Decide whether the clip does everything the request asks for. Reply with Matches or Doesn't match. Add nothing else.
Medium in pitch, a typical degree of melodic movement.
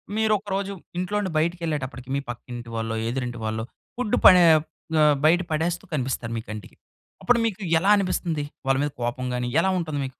Doesn't match